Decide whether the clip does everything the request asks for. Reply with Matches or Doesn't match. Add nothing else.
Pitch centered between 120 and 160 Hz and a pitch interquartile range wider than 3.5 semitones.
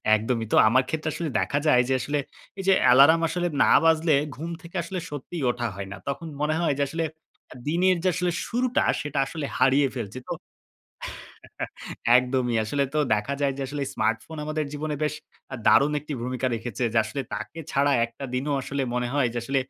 Matches